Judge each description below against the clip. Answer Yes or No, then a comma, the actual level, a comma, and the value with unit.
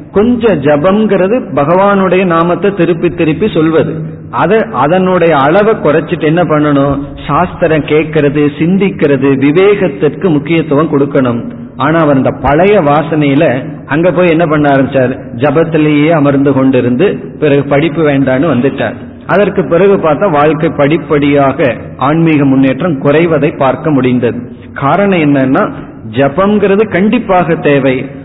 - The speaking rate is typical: Yes, average, 105 wpm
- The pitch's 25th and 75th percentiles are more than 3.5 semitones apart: Yes, average, 3.9 semitones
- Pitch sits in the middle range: Yes, medium, 150 Hz